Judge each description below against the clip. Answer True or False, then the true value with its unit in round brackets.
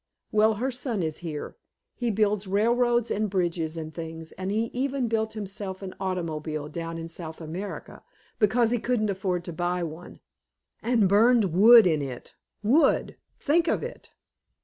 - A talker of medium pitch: False (195 Hz)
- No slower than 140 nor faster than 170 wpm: True (160 wpm)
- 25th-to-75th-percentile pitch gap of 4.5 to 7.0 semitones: True (5.5 semitones)